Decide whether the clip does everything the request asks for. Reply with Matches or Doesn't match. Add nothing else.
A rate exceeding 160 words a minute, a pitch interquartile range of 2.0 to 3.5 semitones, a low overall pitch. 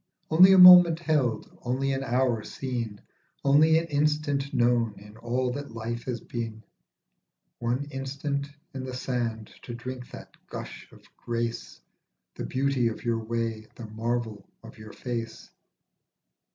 Doesn't match